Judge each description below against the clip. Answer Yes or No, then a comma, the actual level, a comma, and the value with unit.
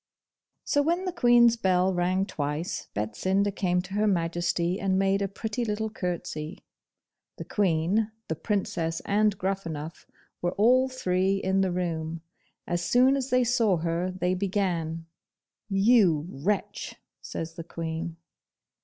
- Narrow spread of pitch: No, average, 3.8 semitones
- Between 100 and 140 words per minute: Yes, slow, 135 wpm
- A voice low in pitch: No, medium, 185 Hz